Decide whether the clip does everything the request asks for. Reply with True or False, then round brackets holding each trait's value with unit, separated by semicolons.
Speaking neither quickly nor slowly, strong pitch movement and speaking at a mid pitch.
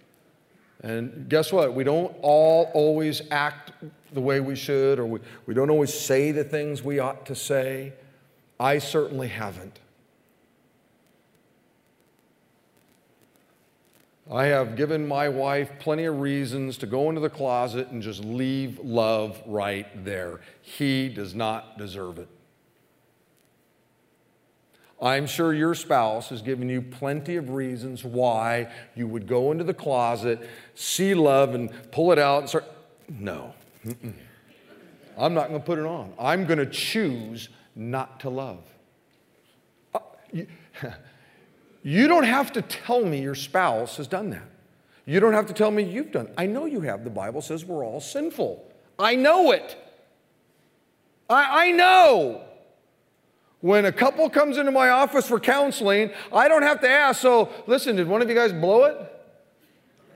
True (150 wpm; 7.4 semitones; 145 Hz)